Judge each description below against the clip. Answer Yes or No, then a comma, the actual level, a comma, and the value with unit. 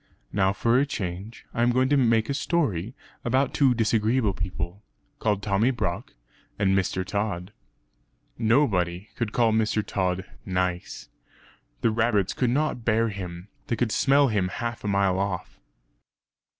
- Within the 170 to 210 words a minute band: No, average, 150 wpm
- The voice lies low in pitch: Yes, low, 110 Hz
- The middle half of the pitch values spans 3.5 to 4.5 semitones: Yes, average, 3.9 semitones